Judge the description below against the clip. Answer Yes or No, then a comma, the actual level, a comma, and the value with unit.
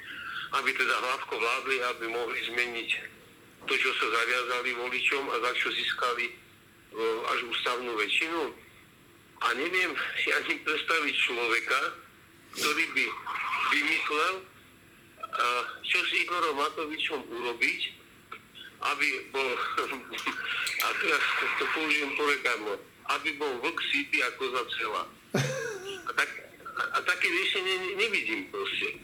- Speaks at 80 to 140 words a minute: Yes, slow, 110 wpm